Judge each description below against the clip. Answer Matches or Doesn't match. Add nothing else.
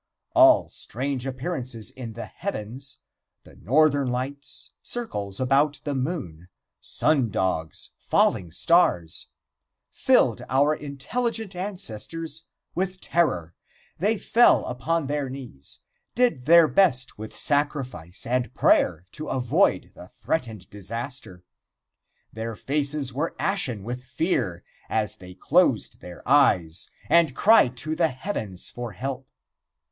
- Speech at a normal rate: Doesn't match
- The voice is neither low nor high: Doesn't match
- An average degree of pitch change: Doesn't match